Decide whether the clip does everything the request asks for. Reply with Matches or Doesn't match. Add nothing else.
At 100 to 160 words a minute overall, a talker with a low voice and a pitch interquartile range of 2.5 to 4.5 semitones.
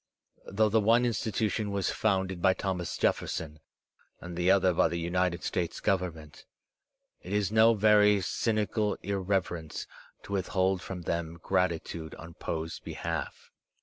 Matches